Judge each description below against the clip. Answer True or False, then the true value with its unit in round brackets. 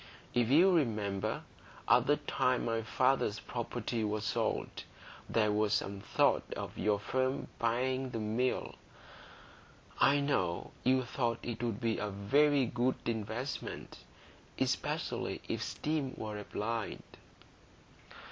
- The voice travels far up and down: False (3.5 semitones)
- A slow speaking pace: True (120 wpm)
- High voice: False (115 Hz)